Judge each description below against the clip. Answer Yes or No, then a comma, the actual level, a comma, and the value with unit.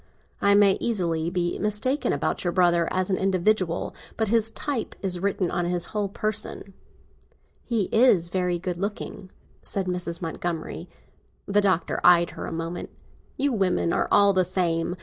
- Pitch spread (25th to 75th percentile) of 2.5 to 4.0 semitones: Yes, average, 2.9 semitones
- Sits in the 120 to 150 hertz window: No, medium, 185 Hz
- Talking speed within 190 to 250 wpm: No, average, 160 wpm